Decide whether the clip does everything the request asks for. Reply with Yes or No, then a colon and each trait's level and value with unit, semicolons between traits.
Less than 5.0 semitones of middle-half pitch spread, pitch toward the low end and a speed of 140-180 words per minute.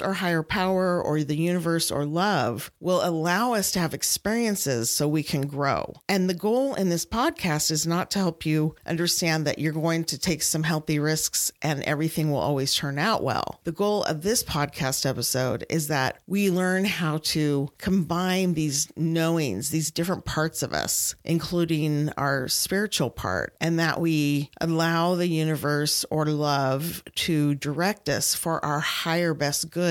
No: average, 3.1 semitones; medium, 160 Hz; average, 170 wpm